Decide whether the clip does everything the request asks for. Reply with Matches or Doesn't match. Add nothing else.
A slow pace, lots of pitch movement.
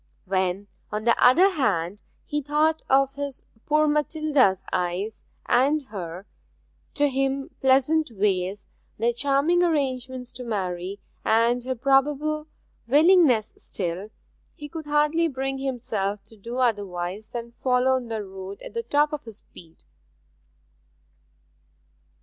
Matches